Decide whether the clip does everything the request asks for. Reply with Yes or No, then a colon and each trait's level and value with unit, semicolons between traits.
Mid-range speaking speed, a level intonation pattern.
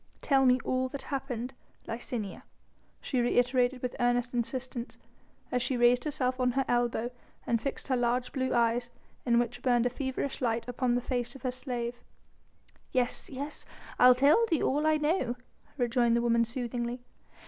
Yes: average, 165 wpm; narrow, 1.4 semitones